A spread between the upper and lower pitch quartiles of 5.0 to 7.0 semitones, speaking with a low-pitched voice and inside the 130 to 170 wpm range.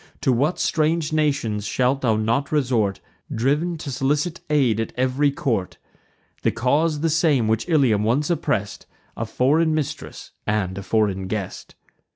Yes: wide, 5.4 semitones; low, 130 Hz; average, 150 wpm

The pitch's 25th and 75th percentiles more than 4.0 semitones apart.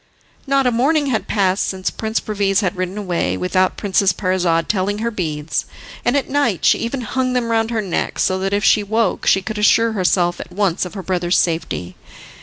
No: average, 3.7 semitones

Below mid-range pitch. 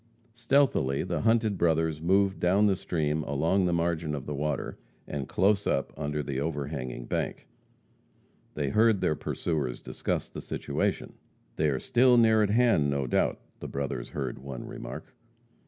Yes: very low, 80 Hz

